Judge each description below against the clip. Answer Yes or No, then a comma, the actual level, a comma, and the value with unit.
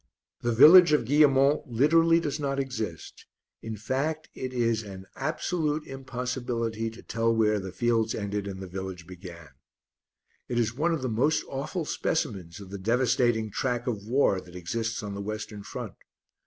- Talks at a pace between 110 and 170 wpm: Yes, average, 165 wpm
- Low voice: Yes, low, 115 Hz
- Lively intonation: No, average, 5.0 semitones